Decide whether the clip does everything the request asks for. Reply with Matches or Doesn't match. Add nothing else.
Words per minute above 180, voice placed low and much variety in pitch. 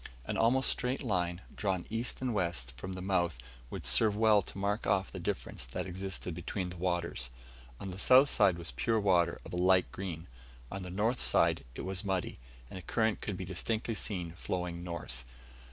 Doesn't match